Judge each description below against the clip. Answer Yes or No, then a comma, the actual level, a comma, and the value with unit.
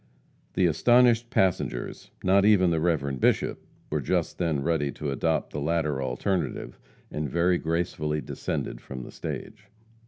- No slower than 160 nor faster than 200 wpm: No, average, 145 wpm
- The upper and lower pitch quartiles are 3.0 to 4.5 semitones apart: Yes, average, 4.0 semitones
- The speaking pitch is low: Yes, very low, 80 Hz